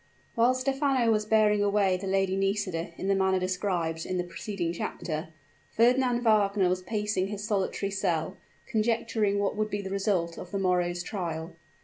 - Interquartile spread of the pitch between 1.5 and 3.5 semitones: Yes, average, 2.8 semitones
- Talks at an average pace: Yes, average, 165 wpm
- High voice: Yes, high, 195 Hz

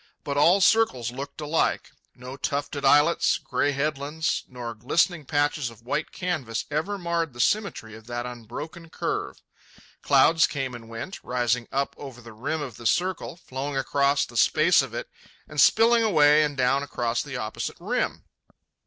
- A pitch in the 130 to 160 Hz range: Yes, medium, 140 Hz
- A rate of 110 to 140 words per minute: No, average, 160 wpm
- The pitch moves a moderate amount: Yes, average, 4.6 semitones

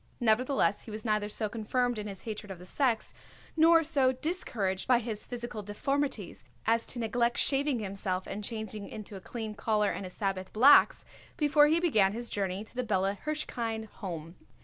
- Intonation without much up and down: No, average, 3.9 semitones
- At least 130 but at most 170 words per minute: No, average, 180 wpm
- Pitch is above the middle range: Yes, high, 220 Hz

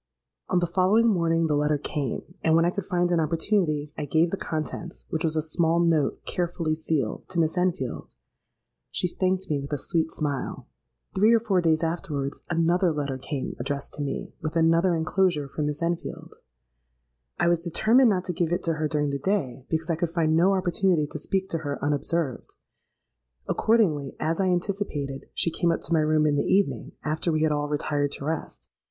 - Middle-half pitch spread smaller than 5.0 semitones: Yes, average, 3.0 semitones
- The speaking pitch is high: No, medium, 165 Hz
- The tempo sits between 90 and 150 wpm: No, average, 195 wpm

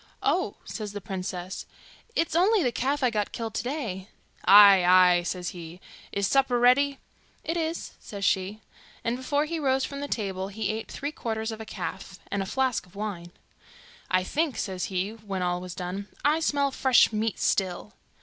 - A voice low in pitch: No, high, 215 Hz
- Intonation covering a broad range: Yes, wide, 6.0 semitones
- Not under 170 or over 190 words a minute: Yes, average, 185 wpm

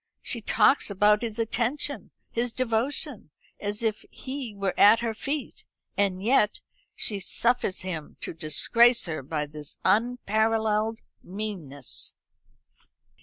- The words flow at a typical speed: No, slow, 120 wpm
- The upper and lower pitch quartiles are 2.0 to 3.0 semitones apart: No, average, 3.7 semitones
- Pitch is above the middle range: Yes, high, 215 Hz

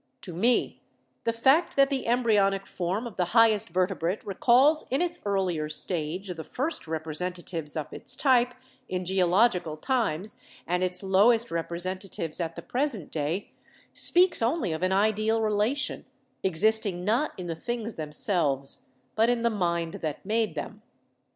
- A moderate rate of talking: Yes, average, 150 wpm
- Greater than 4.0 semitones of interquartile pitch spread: Yes, average, 5.3 semitones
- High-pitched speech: Yes, high, 195 Hz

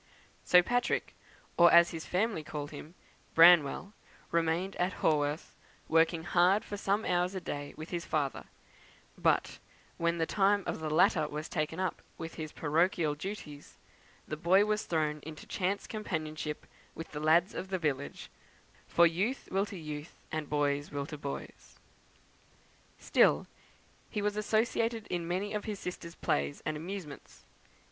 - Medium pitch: Yes, medium, 170 Hz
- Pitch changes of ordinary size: Yes, average, 3.9 semitones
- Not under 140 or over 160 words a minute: Yes, average, 155 wpm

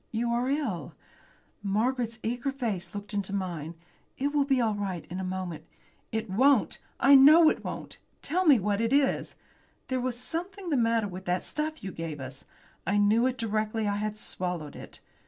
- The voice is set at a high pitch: Yes, high, 220 Hz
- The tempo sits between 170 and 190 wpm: Yes, average, 185 wpm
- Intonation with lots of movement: Yes, wide, 5.7 semitones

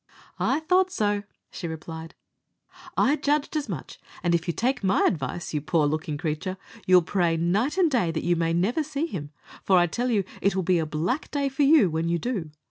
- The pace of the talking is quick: Yes, fast, 215 wpm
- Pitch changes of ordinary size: No, wide, 8.1 semitones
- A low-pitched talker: No, medium, 185 Hz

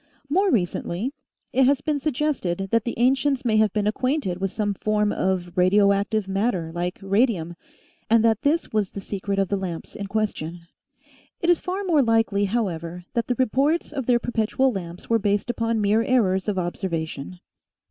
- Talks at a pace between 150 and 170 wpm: No, average, 180 wpm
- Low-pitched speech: No, high, 210 Hz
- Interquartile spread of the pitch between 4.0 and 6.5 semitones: Yes, average, 4.7 semitones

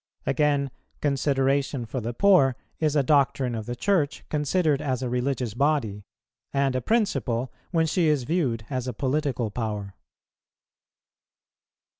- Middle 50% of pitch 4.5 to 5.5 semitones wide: No, average, 3.6 semitones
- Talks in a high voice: No, low, 135 Hz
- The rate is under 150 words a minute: Yes, slow, 135 wpm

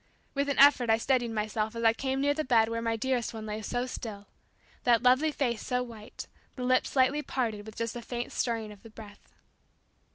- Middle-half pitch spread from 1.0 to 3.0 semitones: Yes, average, 2.7 semitones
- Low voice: No, high, 235 Hz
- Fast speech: Yes, fast, 215 wpm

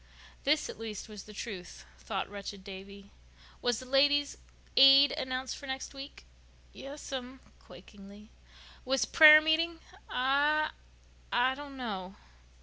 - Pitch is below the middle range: No, very high, 260 Hz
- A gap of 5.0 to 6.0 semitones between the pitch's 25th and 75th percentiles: Yes, wide, 5.4 semitones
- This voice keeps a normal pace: No, slow, 115 wpm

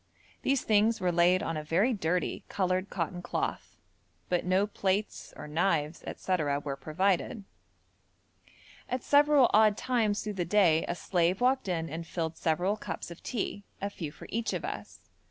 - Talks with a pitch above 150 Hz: Yes, medium, 185 Hz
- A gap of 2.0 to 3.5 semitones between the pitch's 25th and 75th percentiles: No, average, 4.0 semitones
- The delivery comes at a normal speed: Yes, average, 165 wpm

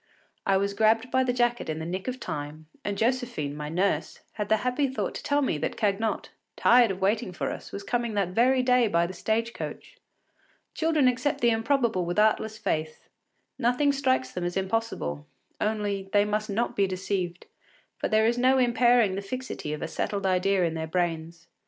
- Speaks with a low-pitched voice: No, high, 210 Hz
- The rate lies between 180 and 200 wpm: Yes, average, 195 wpm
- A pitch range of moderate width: Yes, average, 4.9 semitones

